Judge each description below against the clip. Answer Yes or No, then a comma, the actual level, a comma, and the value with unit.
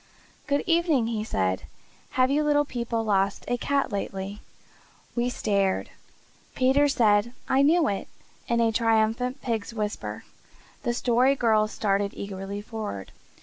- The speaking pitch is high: Yes, high, 230 Hz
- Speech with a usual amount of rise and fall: Yes, average, 4.1 semitones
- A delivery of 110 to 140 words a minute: Yes, slow, 135 wpm